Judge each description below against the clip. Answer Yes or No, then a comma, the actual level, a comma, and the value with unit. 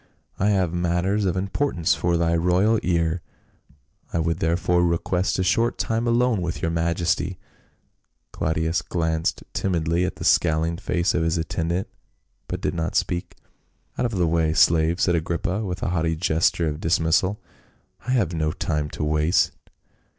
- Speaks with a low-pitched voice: Yes, very low, 85 Hz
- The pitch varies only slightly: Yes, narrow, 2.2 semitones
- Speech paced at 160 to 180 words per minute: Yes, average, 165 wpm